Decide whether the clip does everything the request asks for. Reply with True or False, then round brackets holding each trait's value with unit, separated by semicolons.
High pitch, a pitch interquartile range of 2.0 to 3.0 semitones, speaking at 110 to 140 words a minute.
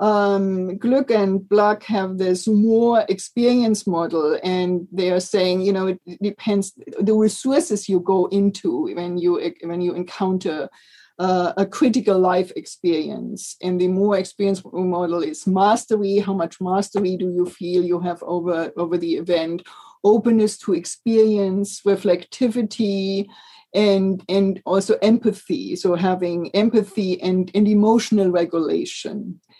True (195 Hz; 2.6 semitones; 135 wpm)